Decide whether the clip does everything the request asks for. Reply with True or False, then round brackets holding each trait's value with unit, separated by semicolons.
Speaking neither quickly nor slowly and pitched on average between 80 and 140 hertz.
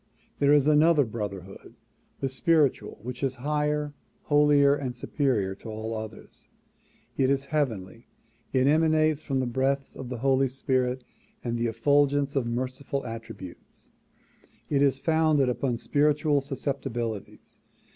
False (130 wpm; 135 Hz)